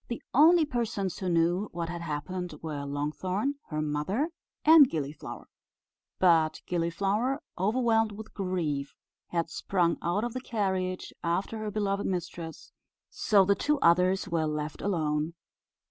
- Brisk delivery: No, slow, 135 wpm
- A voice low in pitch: No, medium, 185 Hz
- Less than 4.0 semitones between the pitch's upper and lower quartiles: No, average, 4.5 semitones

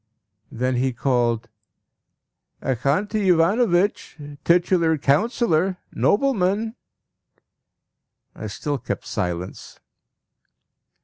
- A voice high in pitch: No, medium, 165 Hz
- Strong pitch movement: Yes, wide, 7.5 semitones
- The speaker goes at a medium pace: No, slow, 65 wpm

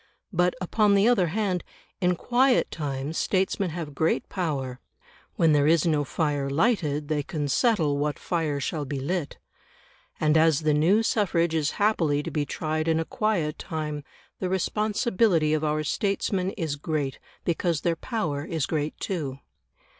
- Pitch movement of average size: Yes, average, 4.0 semitones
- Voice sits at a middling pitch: Yes, medium, 160 Hz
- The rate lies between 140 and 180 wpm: Yes, average, 160 wpm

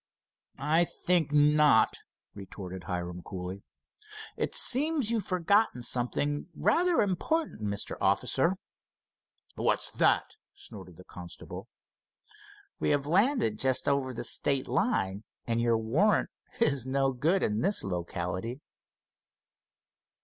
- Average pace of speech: No, slow, 110 wpm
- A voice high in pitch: No, medium, 140 Hz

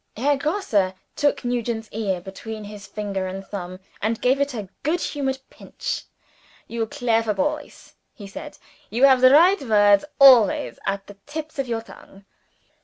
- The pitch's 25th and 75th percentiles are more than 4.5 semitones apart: Yes, average, 5.2 semitones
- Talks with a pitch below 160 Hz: No, high, 225 Hz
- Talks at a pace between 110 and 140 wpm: No, average, 160 wpm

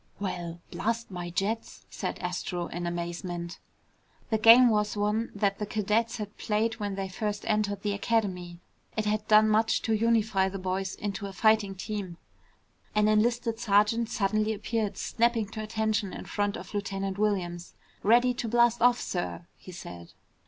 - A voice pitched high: Yes, high, 210 Hz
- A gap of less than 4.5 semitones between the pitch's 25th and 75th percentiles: Yes, narrow, 2.5 semitones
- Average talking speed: Yes, average, 160 wpm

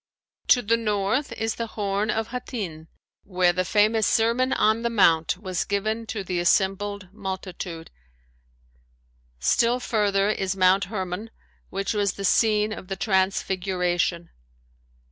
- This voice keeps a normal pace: No, slow, 130 wpm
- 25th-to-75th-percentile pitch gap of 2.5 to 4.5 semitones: Yes, average, 2.9 semitones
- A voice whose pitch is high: Yes, high, 200 Hz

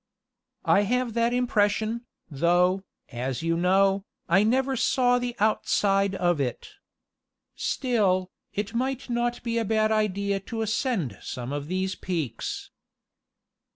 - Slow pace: Yes, slow, 125 wpm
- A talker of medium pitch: No, high, 200 Hz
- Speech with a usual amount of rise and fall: Yes, average, 4.7 semitones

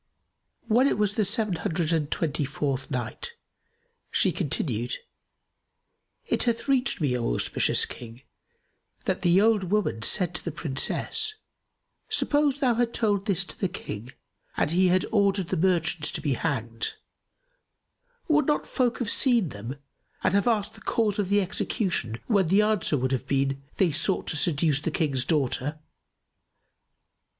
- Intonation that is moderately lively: No, wide, 6.8 semitones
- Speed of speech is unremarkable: Yes, average, 155 wpm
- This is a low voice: No, medium, 180 Hz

